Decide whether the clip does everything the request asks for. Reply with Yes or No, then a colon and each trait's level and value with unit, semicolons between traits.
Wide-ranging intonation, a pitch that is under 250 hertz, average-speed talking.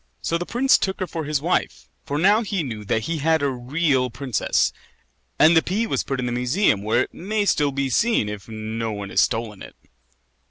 No: wide, 7.2 semitones; medium, 140 Hz; fast, 215 wpm